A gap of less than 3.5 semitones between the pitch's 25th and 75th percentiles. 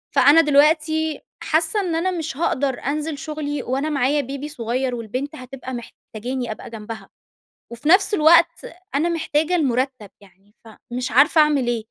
No: average, 4.3 semitones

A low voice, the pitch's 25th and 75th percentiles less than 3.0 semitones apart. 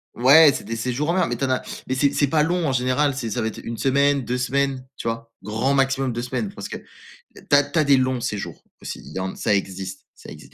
No: low, 130 Hz; average, 3.4 semitones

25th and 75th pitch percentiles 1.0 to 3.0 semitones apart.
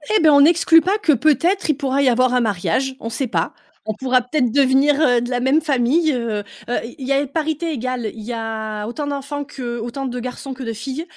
No: average, 3.6 semitones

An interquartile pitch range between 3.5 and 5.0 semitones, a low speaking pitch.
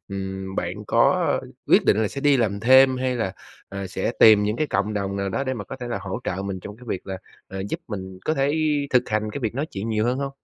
Yes: average, 4.6 semitones; low, 105 Hz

